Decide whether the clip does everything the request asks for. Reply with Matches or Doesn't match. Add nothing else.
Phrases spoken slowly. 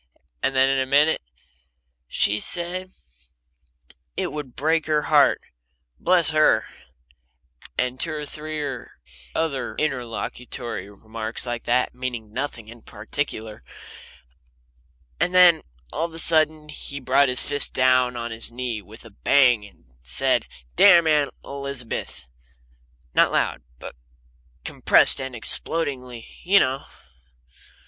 Matches